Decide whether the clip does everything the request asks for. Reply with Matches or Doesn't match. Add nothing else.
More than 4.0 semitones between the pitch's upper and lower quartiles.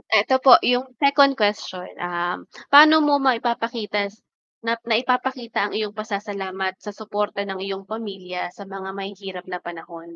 Doesn't match